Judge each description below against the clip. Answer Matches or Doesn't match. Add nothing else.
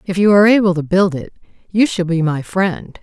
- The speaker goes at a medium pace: Doesn't match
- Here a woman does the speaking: Matches